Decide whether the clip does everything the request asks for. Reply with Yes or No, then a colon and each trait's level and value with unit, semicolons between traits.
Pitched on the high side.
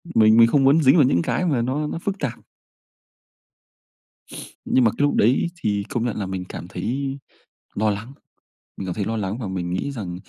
No: low, 115 Hz